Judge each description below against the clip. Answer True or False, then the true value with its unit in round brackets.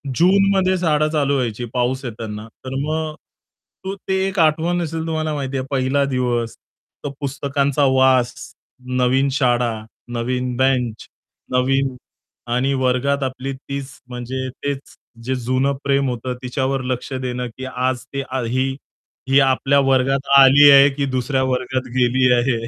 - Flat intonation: True (1.9 semitones)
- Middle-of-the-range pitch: False (130 Hz)